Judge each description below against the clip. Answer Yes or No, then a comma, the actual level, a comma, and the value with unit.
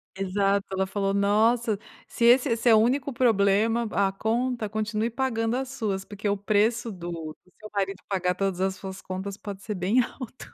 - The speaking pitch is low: No, high, 205 Hz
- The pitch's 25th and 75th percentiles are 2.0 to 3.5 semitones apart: Yes, average, 3.0 semitones